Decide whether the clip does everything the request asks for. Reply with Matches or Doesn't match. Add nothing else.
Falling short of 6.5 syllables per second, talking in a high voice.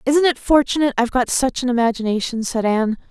Doesn't match